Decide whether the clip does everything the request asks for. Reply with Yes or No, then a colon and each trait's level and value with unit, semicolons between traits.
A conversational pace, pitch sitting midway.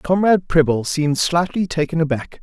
Yes: average, 150 wpm; medium, 160 Hz